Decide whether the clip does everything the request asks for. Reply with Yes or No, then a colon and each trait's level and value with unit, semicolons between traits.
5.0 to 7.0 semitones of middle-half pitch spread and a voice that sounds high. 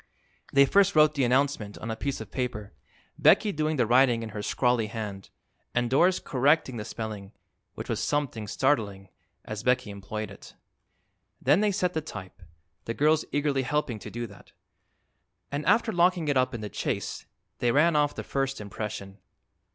No: wide, 5.5 semitones; low, 125 Hz